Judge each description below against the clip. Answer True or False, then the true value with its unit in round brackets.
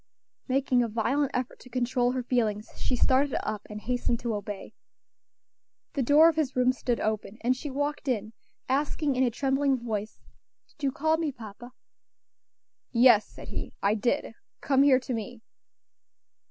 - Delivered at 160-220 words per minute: True (165 wpm)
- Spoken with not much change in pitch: False (3.3 semitones)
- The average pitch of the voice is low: False (250 Hz)